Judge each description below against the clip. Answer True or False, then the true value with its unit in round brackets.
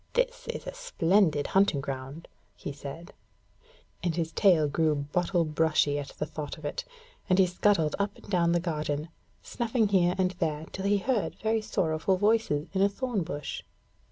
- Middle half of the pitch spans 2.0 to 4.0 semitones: False (4.8 semitones)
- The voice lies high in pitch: False (175 Hz)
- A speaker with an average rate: True (175 wpm)